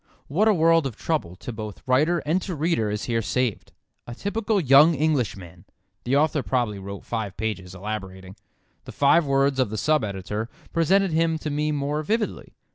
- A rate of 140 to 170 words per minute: No, average, 180 wpm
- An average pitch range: No, wide, 6.9 semitones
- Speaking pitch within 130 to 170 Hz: Yes, low, 135 Hz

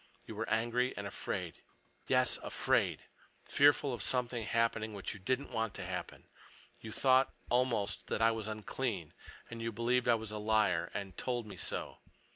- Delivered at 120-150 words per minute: No, average, 165 wpm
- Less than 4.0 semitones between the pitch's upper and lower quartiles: Yes, narrow, 2.6 semitones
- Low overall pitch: Yes, low, 115 Hz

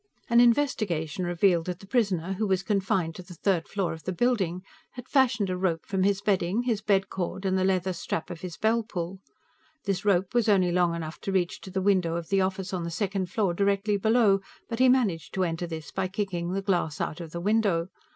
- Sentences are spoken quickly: Yes, fast, 225 wpm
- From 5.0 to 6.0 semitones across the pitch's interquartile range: No, average, 2.7 semitones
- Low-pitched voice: No, high, 190 Hz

